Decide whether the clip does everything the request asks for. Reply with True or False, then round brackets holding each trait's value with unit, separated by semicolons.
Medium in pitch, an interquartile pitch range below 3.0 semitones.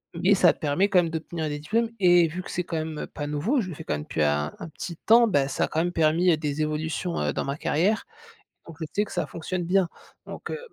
False (165 Hz; 3.3 semitones)